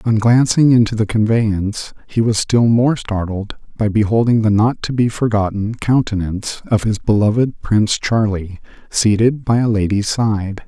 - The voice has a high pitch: No, low, 110 Hz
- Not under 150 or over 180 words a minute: Yes, average, 155 wpm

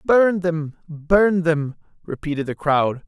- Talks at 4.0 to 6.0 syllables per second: No, 3.5 syllables/s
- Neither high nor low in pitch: Yes, medium, 165 Hz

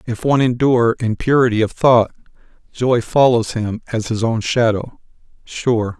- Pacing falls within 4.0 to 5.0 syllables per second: Yes, 4.7 syllables/s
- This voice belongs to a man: Yes, male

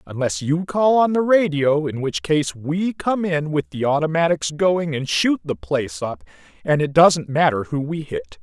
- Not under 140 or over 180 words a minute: No, average, 200 wpm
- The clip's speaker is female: No, male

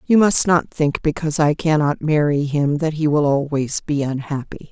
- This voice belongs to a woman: Yes, female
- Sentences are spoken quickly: No, average, 190 wpm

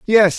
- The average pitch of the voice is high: Yes, high, 205 Hz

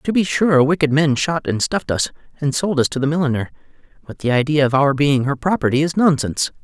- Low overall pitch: No, medium, 145 Hz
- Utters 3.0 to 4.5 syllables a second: No, 6.0 syllables/s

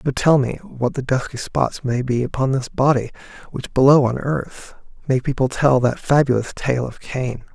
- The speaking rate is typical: Yes, average, 190 wpm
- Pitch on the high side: No, low, 130 Hz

